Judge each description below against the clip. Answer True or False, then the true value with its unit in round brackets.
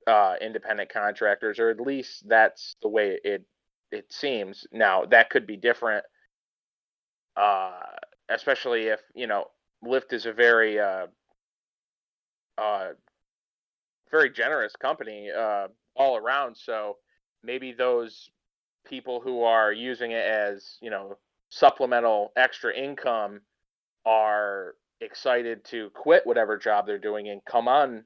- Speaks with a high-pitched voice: False (115 Hz)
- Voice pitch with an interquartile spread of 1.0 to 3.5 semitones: False (4.4 semitones)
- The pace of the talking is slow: True (125 wpm)